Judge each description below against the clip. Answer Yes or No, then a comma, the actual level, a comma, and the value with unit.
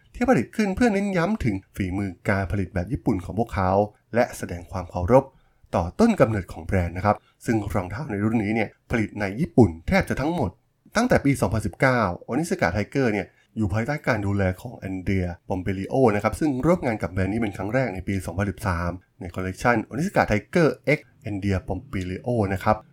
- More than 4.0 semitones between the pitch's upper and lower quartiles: Yes, average, 4.4 semitones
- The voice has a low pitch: Yes, low, 105 Hz